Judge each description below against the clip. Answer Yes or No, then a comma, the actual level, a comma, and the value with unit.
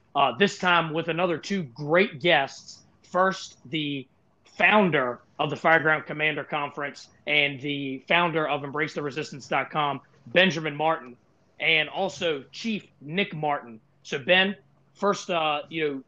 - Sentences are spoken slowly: Yes, slow, 130 wpm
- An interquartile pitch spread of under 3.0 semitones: No, average, 3.6 semitones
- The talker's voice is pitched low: No, medium, 155 Hz